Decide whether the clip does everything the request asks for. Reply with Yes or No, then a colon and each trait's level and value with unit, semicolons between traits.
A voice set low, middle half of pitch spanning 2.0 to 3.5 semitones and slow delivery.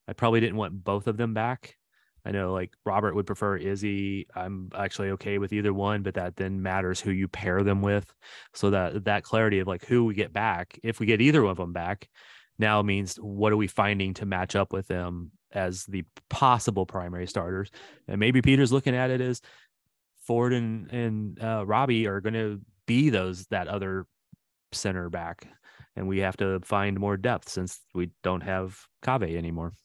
No: low, 100 Hz; average, 2.8 semitones; average, 195 wpm